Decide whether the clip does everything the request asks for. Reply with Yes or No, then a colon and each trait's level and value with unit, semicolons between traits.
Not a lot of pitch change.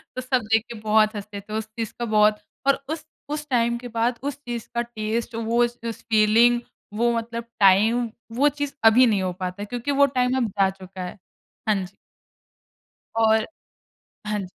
Yes: narrow, 2.3 semitones